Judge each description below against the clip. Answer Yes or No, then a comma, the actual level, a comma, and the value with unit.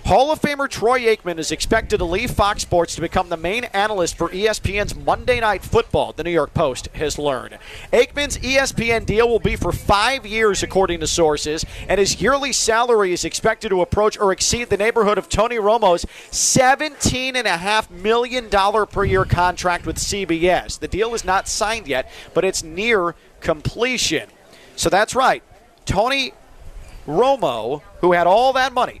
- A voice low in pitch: No, high, 205 Hz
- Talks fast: No, average, 165 wpm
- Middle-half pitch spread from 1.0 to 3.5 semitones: No, average, 5.0 semitones